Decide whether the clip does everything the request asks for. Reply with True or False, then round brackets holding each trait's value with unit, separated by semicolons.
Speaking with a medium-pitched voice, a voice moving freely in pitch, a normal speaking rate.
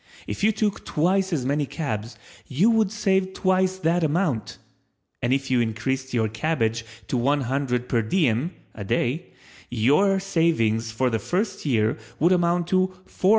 True (145 Hz; 7.8 semitones; 160 wpm)